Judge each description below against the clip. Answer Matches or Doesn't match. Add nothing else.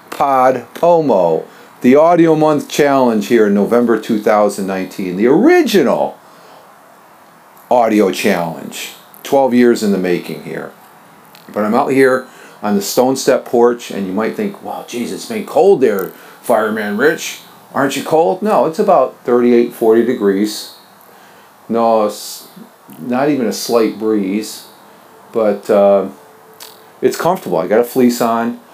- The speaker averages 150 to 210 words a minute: Doesn't match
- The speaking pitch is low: Matches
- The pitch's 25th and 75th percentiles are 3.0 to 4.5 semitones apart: Matches